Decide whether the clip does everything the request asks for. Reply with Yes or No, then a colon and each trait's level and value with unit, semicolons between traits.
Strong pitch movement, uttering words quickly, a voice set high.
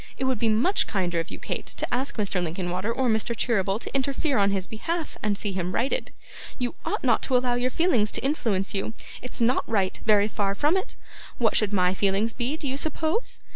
No: average, 4.9 semitones; fast, 215 wpm; high, 225 Hz